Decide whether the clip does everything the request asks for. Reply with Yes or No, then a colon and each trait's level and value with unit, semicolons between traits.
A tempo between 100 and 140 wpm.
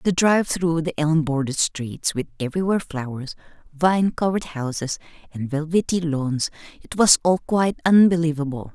Yes: slow, 135 wpm